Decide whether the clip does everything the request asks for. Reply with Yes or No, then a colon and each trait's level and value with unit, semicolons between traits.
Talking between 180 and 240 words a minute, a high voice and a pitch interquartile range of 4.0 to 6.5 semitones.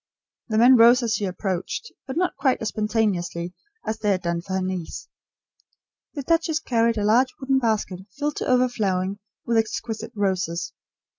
No: average, 165 wpm; high, 220 Hz; average, 5.0 semitones